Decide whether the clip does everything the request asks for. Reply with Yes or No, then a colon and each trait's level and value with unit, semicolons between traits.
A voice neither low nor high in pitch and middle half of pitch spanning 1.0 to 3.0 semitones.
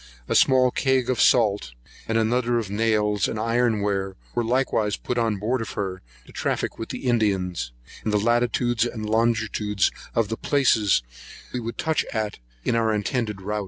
No: low, 110 Hz; narrow, 2.6 semitones